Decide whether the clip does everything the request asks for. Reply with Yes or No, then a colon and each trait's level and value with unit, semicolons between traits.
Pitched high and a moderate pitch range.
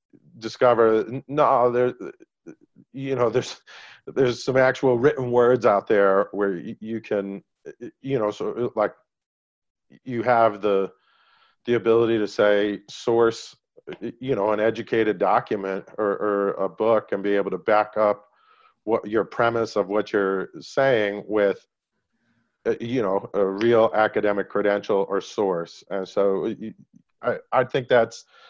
No: low, 110 Hz; average, 3.1 semitones